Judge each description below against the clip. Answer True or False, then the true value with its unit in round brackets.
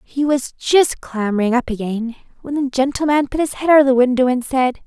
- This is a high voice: True (260 Hz)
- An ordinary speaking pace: False (220 wpm)